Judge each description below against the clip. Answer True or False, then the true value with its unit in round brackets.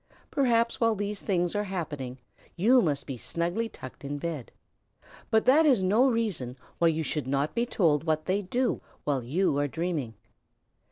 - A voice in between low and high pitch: True (175 Hz)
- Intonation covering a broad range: True (7.4 semitones)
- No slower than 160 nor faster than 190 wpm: True (170 wpm)